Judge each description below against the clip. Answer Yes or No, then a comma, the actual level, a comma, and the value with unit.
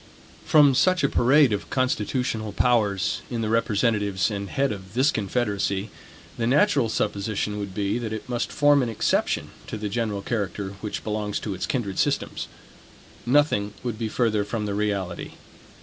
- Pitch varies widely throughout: No, average, 3.3 semitones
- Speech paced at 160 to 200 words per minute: Yes, average, 165 wpm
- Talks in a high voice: No, low, 110 Hz